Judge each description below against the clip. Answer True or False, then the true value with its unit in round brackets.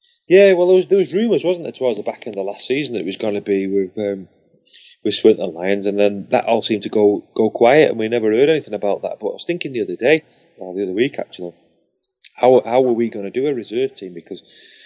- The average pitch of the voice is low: True (115 Hz)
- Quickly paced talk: True (280 wpm)